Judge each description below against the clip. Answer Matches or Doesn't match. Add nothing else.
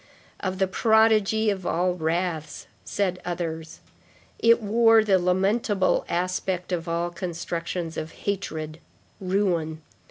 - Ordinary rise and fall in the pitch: Matches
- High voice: Doesn't match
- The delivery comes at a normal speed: Doesn't match